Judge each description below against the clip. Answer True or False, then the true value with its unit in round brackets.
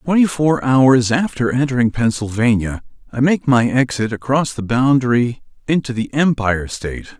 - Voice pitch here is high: False (125 Hz)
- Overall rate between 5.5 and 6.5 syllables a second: False (5.0 syllables/s)